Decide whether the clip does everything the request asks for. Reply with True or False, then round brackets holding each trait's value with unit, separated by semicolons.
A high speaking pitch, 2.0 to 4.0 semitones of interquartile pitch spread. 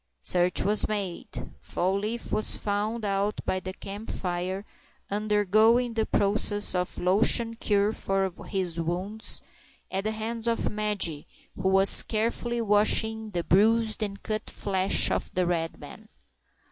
True (205 Hz; 2.6 semitones)